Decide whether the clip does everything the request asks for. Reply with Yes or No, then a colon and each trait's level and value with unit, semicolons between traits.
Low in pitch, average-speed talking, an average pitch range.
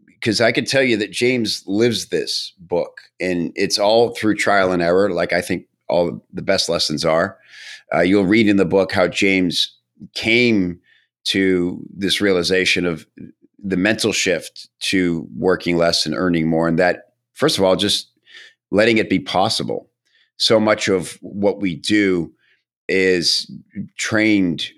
Yes: very low, 95 Hz; average, 155 wpm; average, 3.5 semitones